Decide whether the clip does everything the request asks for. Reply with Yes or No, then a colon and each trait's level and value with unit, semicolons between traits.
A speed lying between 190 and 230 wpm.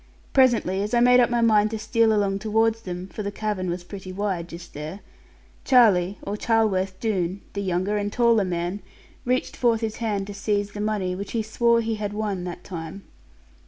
Yes: average, 195 wpm